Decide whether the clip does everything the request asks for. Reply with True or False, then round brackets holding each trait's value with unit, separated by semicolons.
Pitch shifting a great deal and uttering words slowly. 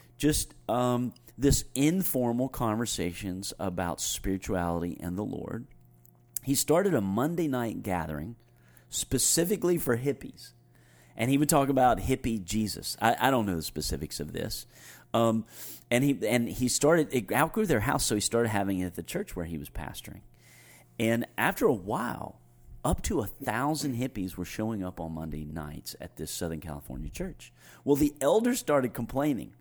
False (7.6 semitones; 165 wpm)